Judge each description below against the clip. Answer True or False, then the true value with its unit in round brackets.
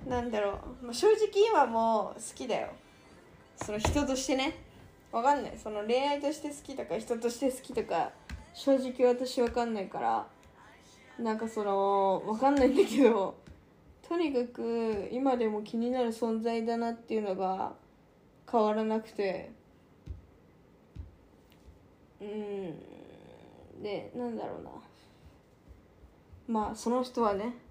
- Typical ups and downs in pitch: True (3.4 semitones)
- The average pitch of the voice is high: True (230 Hz)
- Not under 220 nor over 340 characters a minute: True (245 characters per minute)